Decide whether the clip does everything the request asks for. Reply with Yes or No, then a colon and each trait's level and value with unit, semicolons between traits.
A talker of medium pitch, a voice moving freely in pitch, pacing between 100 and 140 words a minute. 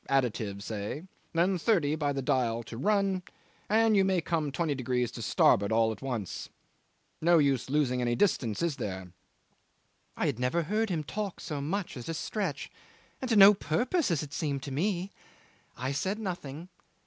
No: medium, 150 Hz; wide, 6.9 semitones; average, 170 wpm